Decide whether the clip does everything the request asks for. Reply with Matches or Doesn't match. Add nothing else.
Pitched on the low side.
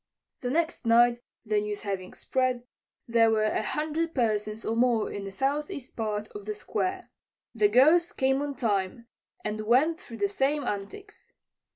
Doesn't match